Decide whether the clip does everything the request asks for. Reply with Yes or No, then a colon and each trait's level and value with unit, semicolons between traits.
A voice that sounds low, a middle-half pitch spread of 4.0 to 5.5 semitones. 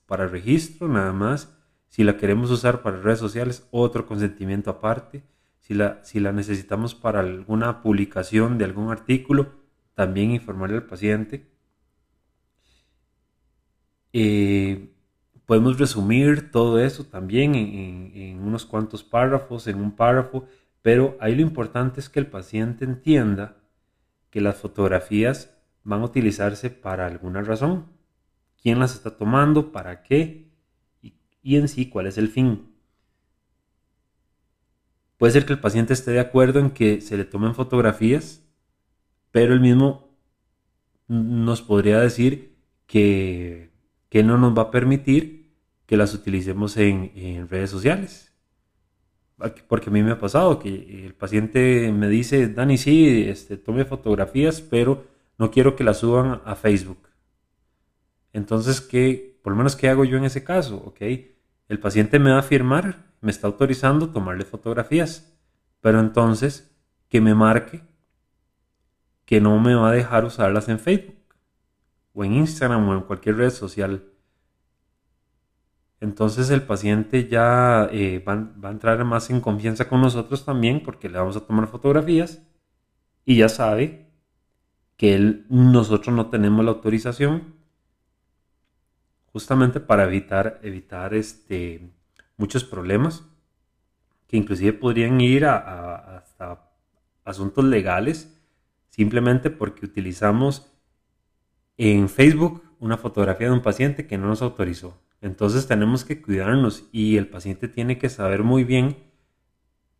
Yes: low, 110 Hz; average, 4.6 semitones